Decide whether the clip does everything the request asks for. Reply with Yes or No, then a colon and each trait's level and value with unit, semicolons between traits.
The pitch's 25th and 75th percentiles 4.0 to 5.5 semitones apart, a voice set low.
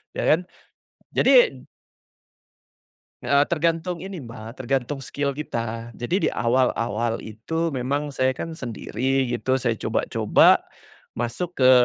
Yes: average, 4.5 semitones; low, 130 Hz